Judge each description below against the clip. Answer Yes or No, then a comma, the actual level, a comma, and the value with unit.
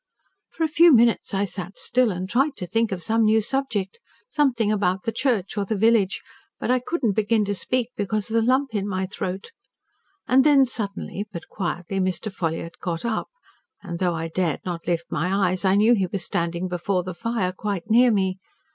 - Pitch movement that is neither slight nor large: Yes, average, 3.9 semitones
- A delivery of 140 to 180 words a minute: No, fast, 205 wpm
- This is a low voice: No, high, 205 Hz